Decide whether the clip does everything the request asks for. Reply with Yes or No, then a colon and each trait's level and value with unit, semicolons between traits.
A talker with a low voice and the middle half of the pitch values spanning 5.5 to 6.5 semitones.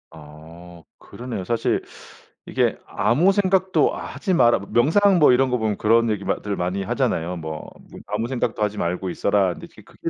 Yes: low, 105 Hz; wide, 6.0 semitones